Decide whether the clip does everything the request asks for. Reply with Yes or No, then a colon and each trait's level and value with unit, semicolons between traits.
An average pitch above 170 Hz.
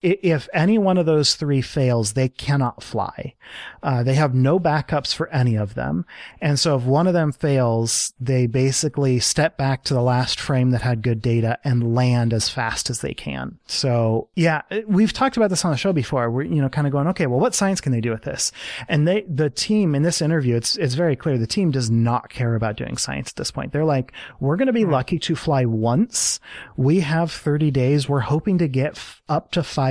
No: medium, 140 Hz